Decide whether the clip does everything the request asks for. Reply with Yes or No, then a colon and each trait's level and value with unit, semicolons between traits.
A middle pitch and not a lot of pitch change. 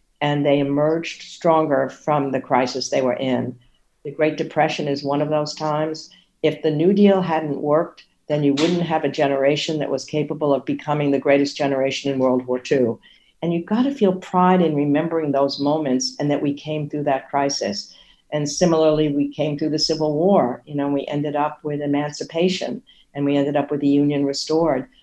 Yes: medium, 150 Hz; narrow, 1.9 semitones